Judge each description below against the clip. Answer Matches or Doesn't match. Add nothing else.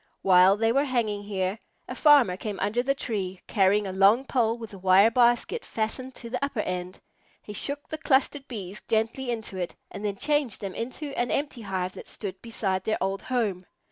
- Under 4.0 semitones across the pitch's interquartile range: Doesn't match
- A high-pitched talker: Matches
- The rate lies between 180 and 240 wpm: Matches